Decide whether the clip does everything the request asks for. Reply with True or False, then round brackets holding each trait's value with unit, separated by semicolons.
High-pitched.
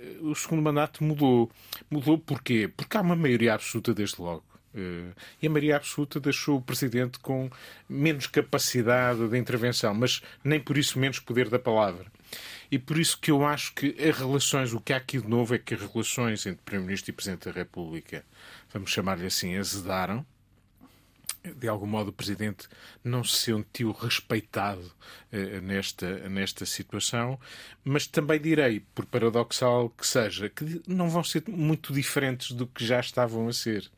False (120 Hz)